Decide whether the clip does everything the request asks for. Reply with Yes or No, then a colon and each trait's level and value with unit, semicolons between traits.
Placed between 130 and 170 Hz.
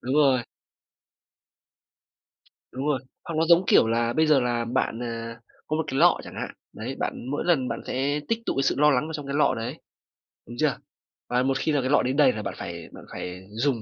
Yes: low, 135 Hz